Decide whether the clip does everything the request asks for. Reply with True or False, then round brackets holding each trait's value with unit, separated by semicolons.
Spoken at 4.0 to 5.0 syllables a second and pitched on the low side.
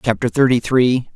True (4.8 syllables/s; 115 Hz)